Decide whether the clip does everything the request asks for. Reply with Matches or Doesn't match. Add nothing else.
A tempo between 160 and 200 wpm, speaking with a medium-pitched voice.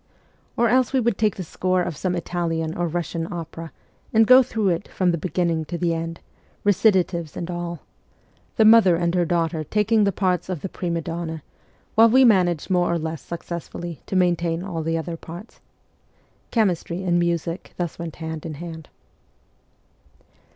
Matches